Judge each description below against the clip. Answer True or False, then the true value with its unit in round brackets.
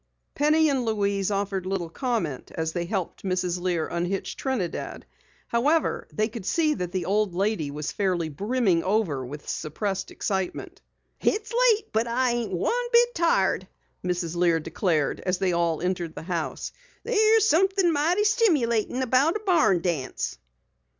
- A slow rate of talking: False (150 wpm)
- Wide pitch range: True (8.7 semitones)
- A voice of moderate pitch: False (200 Hz)